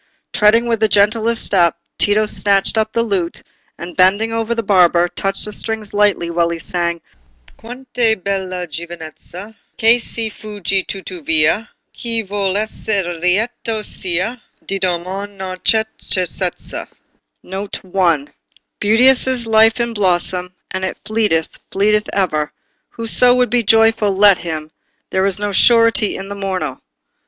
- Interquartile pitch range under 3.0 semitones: No, average, 3.5 semitones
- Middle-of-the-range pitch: No, high, 200 Hz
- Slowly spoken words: Yes, slow, 130 wpm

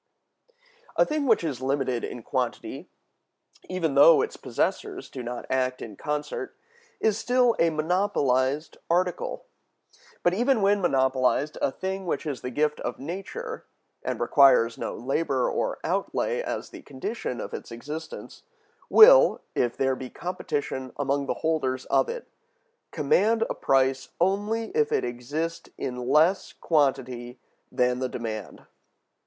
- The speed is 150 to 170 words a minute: No, average, 140 wpm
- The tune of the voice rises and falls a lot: Yes, wide, 7.1 semitones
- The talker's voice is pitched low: No, medium, 150 Hz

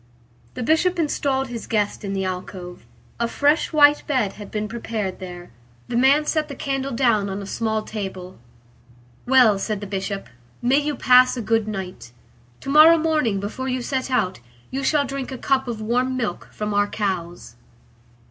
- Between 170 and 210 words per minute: Yes, average, 175 wpm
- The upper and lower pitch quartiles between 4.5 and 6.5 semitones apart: Yes, average, 5.1 semitones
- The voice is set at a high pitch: Yes, high, 235 Hz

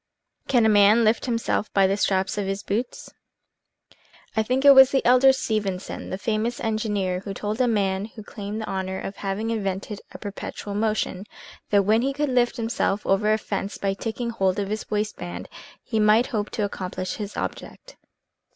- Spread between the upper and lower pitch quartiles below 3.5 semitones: Yes, narrow, 2.6 semitones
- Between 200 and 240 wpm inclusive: No, average, 185 wpm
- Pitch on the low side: No, high, 210 Hz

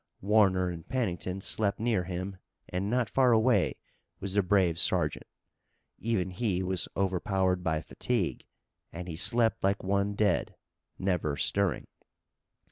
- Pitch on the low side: Yes, very low, 95 Hz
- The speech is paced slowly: Yes, slow, 130 wpm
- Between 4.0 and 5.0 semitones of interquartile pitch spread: No, average, 2.7 semitones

